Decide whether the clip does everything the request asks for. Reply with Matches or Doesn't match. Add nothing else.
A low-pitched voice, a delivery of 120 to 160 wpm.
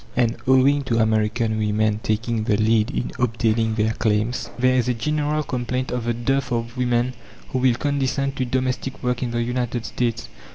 Doesn't match